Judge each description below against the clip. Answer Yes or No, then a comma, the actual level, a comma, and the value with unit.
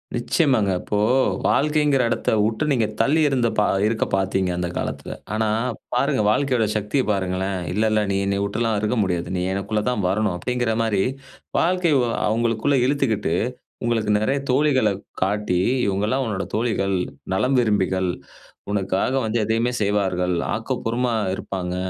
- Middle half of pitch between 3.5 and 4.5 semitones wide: Yes, average, 3.9 semitones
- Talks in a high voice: No, low, 110 Hz